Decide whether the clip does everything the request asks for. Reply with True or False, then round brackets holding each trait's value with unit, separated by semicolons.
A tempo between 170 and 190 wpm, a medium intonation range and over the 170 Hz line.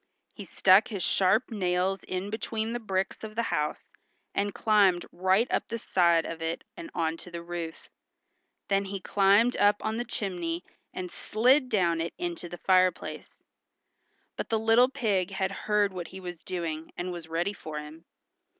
True (175 wpm; 3.8 semitones; 190 Hz)